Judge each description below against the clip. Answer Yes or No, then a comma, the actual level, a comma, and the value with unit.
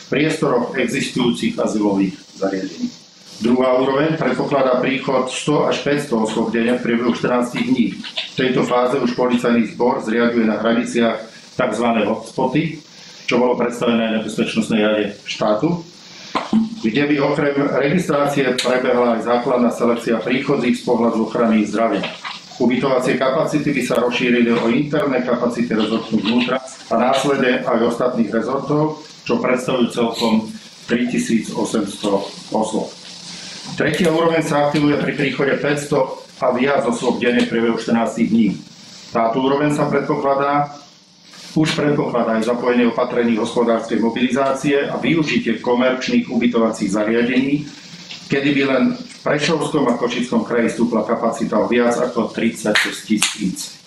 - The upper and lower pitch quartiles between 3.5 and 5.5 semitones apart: Yes, average, 3.9 semitones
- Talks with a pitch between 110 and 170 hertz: Yes, low, 125 Hz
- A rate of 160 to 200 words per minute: No, average, 125 wpm